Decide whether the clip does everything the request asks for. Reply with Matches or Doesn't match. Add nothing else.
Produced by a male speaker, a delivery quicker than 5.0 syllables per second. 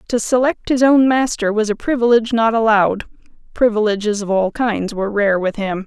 Doesn't match